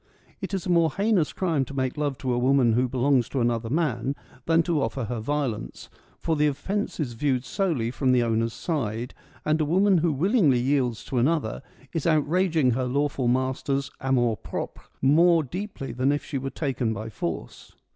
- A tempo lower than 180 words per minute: No, average, 190 wpm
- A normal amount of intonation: Yes, average, 4.6 semitones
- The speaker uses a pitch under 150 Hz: Yes, low, 135 Hz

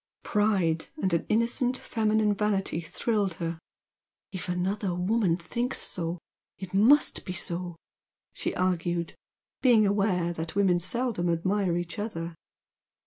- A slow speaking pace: Yes, slow, 125 wpm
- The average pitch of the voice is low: No, high, 190 Hz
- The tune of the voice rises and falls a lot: No, average, 3.6 semitones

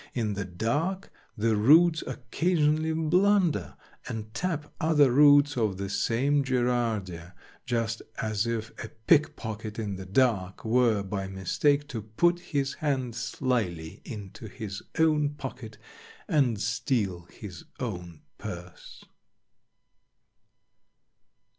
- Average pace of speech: No, slow, 110 wpm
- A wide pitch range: Yes, wide, 6.1 semitones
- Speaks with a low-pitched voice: Yes, low, 115 Hz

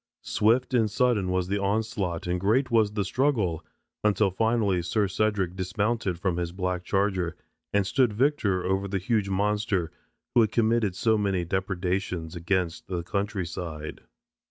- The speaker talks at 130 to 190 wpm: Yes, average, 155 wpm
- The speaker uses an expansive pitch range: No, average, 3.1 semitones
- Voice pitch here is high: No, low, 100 Hz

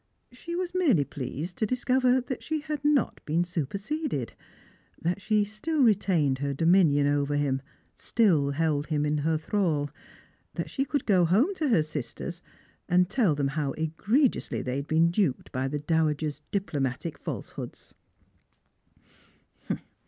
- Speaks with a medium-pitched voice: Yes, medium, 170 Hz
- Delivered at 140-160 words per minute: Yes, average, 145 wpm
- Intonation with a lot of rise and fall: Yes, wide, 8.0 semitones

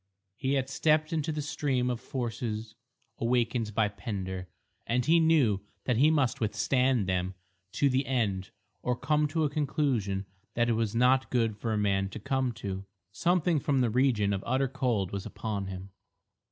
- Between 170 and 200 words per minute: Yes, average, 175 wpm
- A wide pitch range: No, average, 4.7 semitones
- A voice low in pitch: Yes, low, 120 Hz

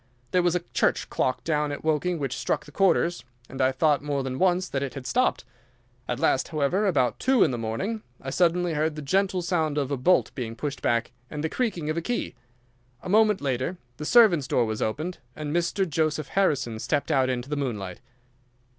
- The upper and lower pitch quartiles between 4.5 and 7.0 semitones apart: Yes, average, 5.1 semitones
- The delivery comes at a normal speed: No, fast, 210 wpm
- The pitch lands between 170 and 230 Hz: No, medium, 150 Hz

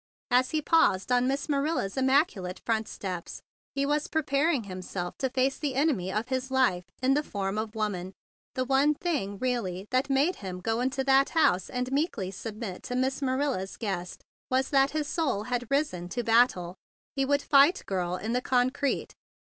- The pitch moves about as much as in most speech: No, wide, 5.9 semitones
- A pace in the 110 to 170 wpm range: No, average, 190 wpm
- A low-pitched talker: No, very high, 255 Hz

